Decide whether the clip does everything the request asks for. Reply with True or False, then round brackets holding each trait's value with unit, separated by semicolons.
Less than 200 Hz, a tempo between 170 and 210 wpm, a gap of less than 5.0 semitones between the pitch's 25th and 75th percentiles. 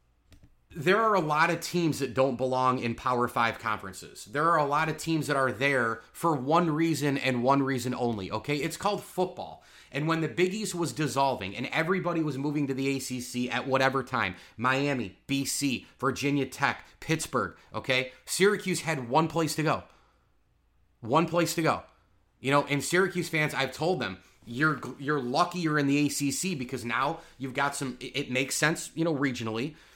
True (140 Hz; 185 wpm; 4.0 semitones)